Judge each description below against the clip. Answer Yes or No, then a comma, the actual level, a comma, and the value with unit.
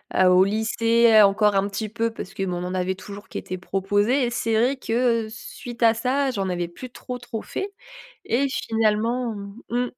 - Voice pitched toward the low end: No, high, 225 Hz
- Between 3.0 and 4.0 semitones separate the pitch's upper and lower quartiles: Yes, average, 3.4 semitones